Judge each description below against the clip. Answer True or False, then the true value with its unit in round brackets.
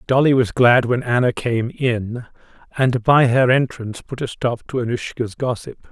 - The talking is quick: False (175 wpm)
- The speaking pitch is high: False (125 Hz)